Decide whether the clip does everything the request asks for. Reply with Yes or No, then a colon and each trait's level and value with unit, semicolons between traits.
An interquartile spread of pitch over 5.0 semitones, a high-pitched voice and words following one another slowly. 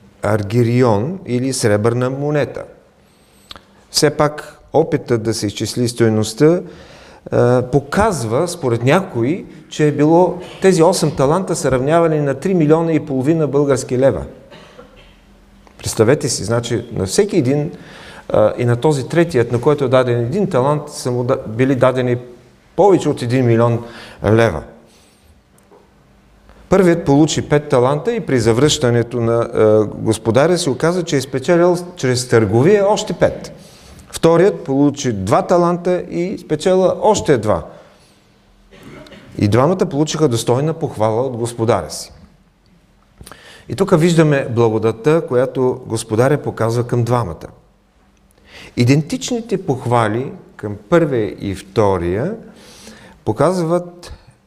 No: wide, 5.6 semitones; low, 135 Hz; slow, 115 wpm